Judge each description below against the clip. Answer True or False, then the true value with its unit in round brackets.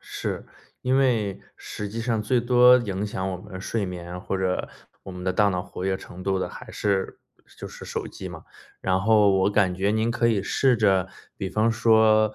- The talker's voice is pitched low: True (100 Hz)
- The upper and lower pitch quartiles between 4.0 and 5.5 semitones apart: False (3.0 semitones)